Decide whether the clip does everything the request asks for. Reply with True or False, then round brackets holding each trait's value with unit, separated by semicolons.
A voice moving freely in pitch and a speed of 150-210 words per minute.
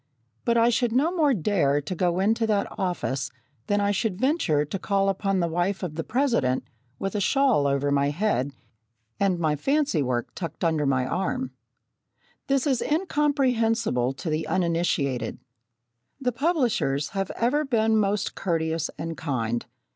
True (7.8 semitones; 155 wpm)